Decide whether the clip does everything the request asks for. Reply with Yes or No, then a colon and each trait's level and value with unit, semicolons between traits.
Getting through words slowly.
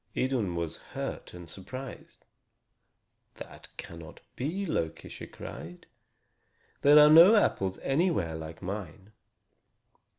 Yes: slow, 105 wpm